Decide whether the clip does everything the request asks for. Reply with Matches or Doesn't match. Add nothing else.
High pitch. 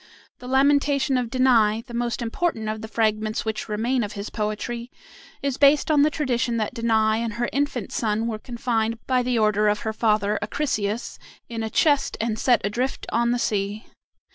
Matches